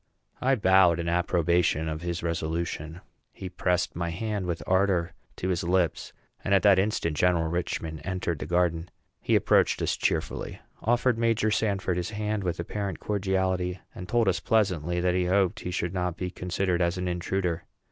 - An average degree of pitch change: No, narrow, 2.1 semitones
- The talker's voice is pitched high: No, very low, 90 Hz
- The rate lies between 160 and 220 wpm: Yes, average, 175 wpm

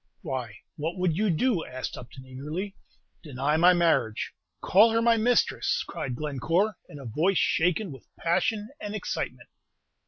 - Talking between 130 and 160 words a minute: Yes, average, 150 wpm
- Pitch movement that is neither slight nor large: No, wide, 7.2 semitones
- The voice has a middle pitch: Yes, medium, 165 Hz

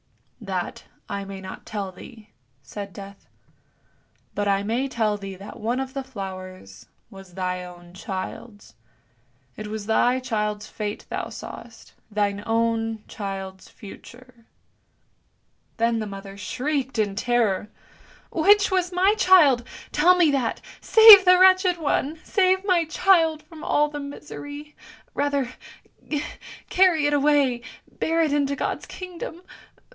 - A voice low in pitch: No, high, 240 Hz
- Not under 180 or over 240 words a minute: No, slow, 135 wpm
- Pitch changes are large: Yes, wide, 7.2 semitones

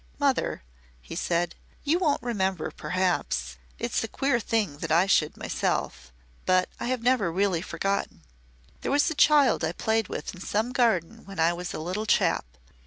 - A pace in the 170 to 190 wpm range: Yes, average, 175 wpm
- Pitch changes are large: Yes, wide, 6.1 semitones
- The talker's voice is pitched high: Yes, high, 195 Hz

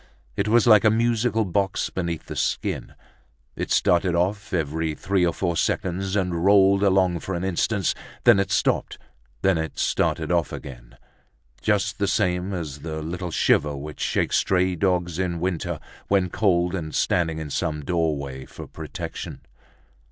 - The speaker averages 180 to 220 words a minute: No, average, 160 wpm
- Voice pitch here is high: No, very low, 90 Hz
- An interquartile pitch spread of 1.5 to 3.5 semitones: Yes, average, 3.1 semitones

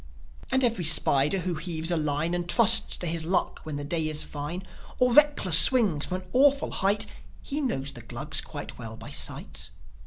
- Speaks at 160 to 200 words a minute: Yes, average, 190 wpm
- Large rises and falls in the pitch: Yes, wide, 6.3 semitones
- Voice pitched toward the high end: No, medium, 170 Hz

